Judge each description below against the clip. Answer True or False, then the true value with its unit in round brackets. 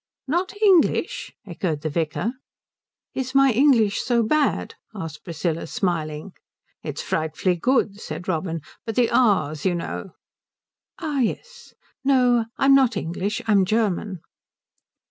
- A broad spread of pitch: True (7.5 semitones)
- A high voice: True (215 Hz)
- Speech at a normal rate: False (125 wpm)